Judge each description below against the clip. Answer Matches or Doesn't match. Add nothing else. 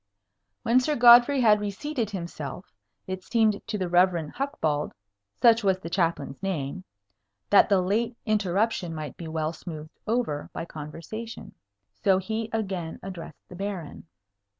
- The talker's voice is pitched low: Doesn't match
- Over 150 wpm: Doesn't match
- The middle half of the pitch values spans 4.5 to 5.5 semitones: Matches